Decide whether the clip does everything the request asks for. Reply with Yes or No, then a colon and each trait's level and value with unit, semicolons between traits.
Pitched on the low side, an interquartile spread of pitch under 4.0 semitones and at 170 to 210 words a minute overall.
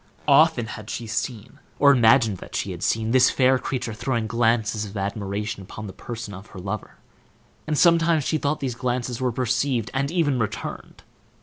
Yes: low, 120 Hz; average, 3.6 semitones; average, 180 wpm